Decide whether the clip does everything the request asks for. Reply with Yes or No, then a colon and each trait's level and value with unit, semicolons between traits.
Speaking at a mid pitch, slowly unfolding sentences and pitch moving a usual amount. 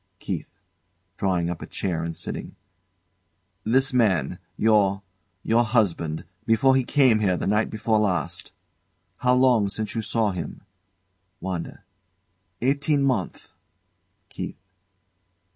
No: low, 110 Hz; slow, 115 wpm; average, 4.9 semitones